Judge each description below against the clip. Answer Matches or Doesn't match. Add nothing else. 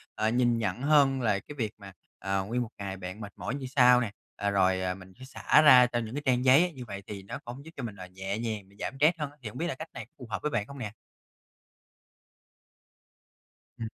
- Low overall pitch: Matches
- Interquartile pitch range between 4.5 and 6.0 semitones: Matches